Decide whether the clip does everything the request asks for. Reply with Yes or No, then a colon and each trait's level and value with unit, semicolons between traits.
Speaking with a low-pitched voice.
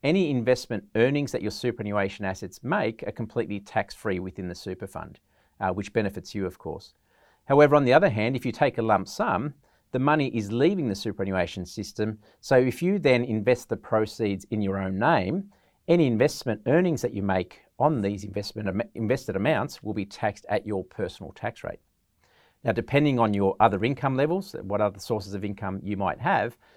Yes: low, 110 Hz